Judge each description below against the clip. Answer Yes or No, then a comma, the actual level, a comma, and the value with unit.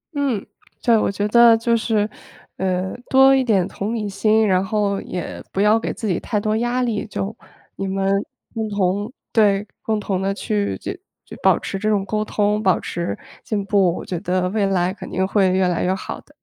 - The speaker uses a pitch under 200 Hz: No, high, 205 Hz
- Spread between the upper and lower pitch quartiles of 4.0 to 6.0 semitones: No, narrow, 2.4 semitones